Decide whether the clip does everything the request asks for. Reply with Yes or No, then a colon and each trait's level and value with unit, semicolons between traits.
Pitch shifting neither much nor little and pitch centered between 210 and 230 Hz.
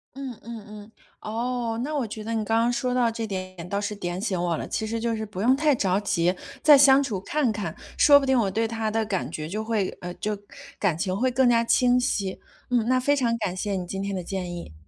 Yes: average, 4.2 semitones; high, 220 Hz